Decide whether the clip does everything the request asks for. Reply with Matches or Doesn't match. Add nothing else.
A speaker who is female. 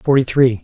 Doesn't match